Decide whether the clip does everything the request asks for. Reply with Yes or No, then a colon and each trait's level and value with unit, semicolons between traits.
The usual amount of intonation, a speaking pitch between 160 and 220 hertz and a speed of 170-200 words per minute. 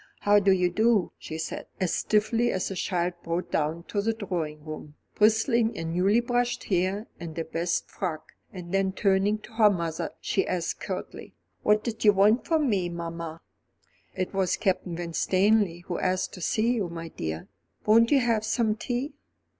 Yes: average, 4.2 semitones; high, 190 Hz; average, 180 wpm